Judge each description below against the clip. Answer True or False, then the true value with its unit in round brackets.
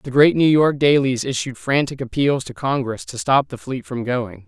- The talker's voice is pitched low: True (130 Hz)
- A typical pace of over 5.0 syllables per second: False (4.7 syllables/s)